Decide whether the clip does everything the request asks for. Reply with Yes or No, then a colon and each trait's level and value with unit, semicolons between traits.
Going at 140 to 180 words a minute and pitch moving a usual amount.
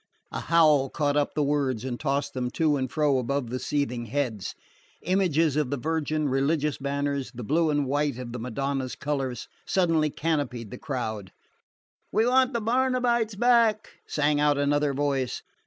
Yes: average, 165 wpm; average, 3.4 semitones